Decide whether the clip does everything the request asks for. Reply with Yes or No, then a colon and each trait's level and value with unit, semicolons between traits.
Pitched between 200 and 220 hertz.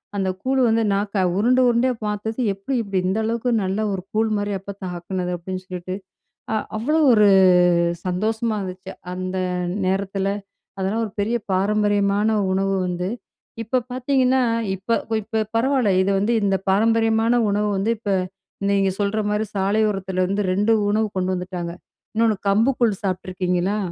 Yes: high, 205 Hz